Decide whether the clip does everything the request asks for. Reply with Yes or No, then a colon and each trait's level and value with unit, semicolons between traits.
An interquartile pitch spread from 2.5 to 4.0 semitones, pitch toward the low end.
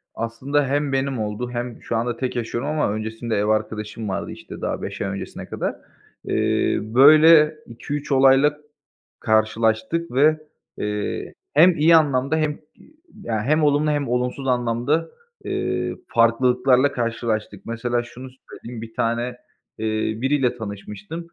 No: average, 4.4 semitones; low, 125 Hz